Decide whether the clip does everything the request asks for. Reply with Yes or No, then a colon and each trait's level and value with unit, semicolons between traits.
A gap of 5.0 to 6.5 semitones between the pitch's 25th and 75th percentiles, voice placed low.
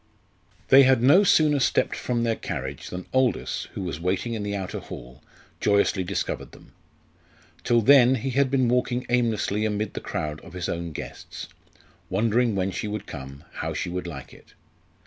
Yes: wide, 5.5 semitones; low, 105 Hz